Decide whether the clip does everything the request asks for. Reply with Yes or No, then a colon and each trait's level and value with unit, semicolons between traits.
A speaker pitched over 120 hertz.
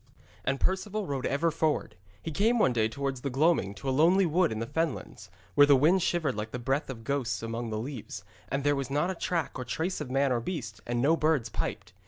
Yes: medium, 140 Hz